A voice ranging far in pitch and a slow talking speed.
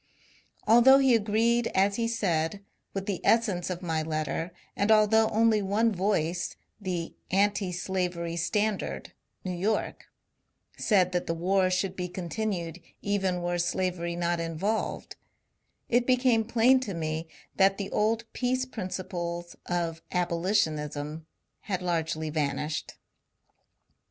No: average, 3.9 semitones; slow, 130 wpm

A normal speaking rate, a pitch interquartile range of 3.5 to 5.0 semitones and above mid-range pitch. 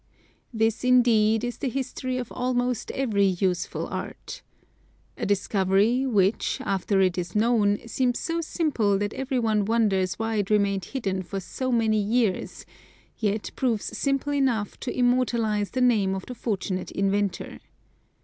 Yes: average, 145 wpm; average, 4.0 semitones; high, 220 Hz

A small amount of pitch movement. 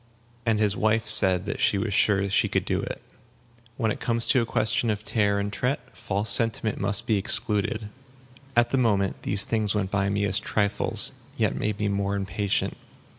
Yes: narrow, 1.8 semitones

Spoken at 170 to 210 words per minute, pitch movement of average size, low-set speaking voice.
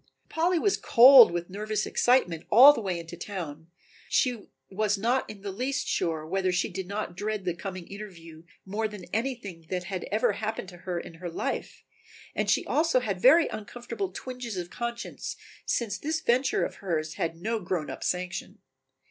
No: average, 180 wpm; average, 5.0 semitones; high, 200 Hz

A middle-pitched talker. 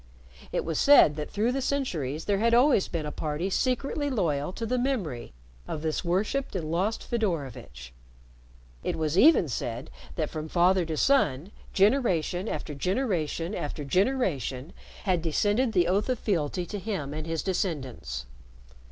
Yes: medium, 180 Hz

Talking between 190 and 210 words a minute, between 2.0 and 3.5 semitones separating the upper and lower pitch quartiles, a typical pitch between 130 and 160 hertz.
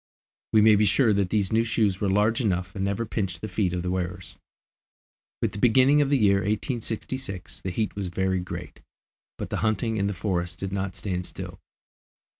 No: average, 200 wpm; average, 2.8 semitones; low, 100 Hz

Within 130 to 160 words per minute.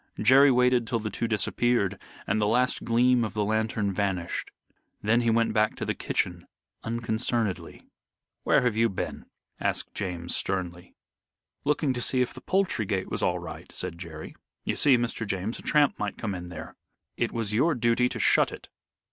No: average, 180 wpm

